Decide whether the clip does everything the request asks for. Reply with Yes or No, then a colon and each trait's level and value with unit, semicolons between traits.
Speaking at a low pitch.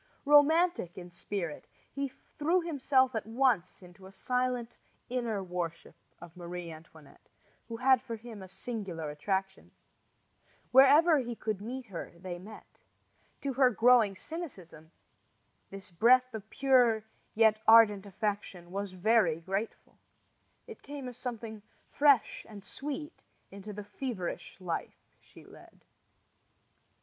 No: high, 220 Hz